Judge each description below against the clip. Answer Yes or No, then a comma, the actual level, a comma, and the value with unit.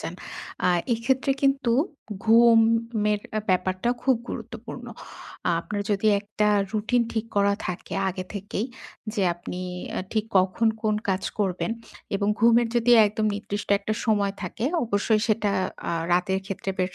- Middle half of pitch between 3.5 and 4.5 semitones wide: No, average, 2.7 semitones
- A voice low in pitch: No, high, 210 Hz